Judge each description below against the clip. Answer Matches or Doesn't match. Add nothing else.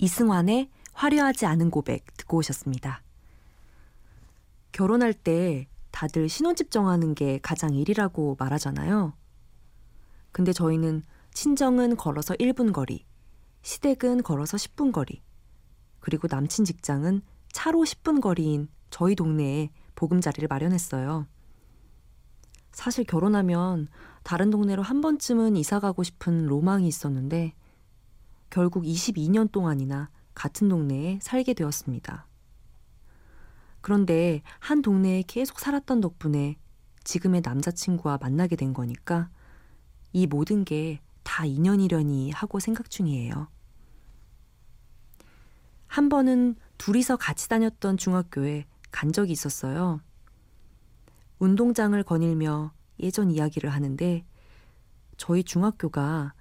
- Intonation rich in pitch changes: Matches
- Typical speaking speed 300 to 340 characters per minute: Doesn't match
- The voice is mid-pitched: Matches